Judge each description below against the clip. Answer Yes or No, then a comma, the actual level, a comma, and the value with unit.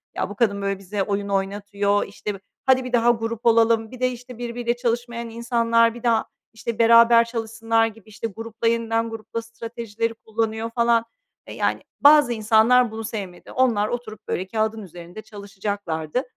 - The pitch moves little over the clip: Yes, narrow, 2.1 semitones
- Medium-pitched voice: No, high, 225 Hz